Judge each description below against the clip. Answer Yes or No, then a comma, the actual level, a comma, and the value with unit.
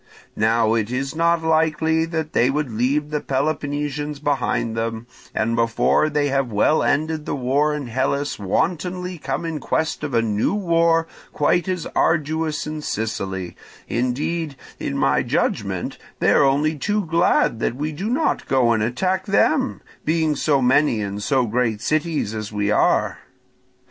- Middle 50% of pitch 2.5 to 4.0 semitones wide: No, average, 5.3 semitones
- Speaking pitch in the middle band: Yes, medium, 145 Hz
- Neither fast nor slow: Yes, average, 160 wpm